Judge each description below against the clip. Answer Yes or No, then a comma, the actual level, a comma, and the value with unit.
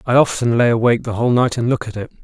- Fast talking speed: Yes, fast, 295 wpm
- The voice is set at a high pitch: No, low, 120 Hz